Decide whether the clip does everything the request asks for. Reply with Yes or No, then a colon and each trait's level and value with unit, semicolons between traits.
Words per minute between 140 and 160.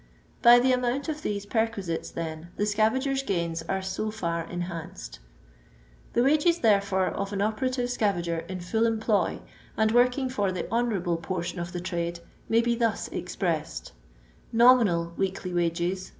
Yes: average, 155 wpm